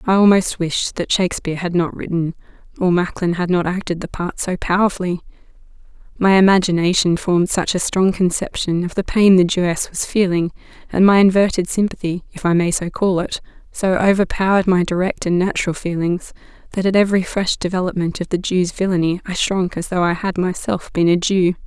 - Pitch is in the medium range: Yes, medium, 180 Hz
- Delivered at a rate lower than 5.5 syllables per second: No, 5.6 syllables/s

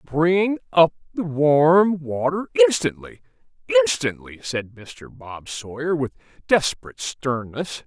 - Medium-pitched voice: Yes, medium, 155 Hz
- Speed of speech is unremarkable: No, slow, 100 wpm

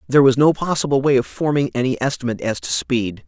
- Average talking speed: No, fast, 220 wpm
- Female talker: No, male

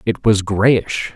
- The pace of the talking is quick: No, average, 155 wpm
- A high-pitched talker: No, low, 105 Hz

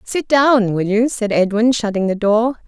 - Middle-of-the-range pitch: No, high, 220 Hz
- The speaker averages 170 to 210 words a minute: Yes, average, 200 wpm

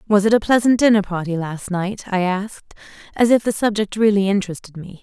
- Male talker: No, female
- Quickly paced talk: No, average, 190 wpm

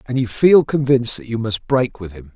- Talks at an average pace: No, fast, 255 wpm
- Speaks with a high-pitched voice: No, low, 120 Hz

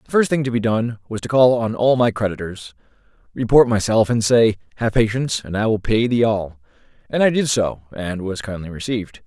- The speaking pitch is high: No, low, 110 Hz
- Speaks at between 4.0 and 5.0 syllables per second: No, 5.5 syllables/s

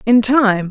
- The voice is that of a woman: Yes, female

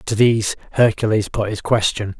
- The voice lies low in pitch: Yes, low, 110 Hz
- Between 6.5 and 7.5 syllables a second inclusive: No, 5.4 syllables/s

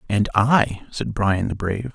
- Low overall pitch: Yes, low, 105 Hz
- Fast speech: No, average, 185 wpm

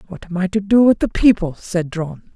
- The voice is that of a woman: Yes, female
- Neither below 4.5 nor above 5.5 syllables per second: Yes, 5.4 syllables/s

